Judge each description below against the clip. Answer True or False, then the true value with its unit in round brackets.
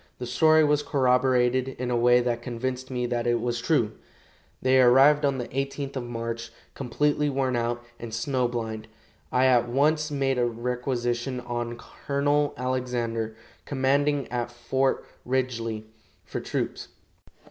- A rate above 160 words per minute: False (145 wpm)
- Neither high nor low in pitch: False (125 Hz)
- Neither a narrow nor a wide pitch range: False (2.2 semitones)